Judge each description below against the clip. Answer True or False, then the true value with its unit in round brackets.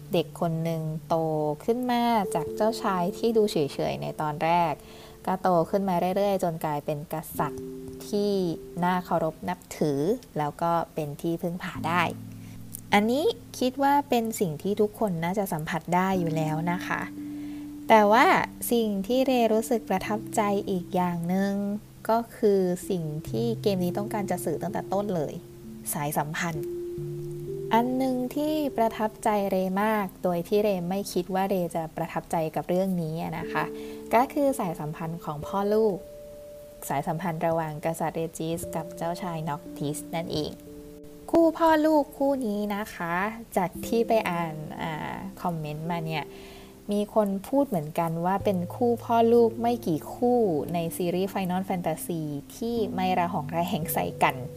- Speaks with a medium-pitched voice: True (180 Hz)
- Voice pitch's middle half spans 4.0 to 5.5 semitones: True (5.1 semitones)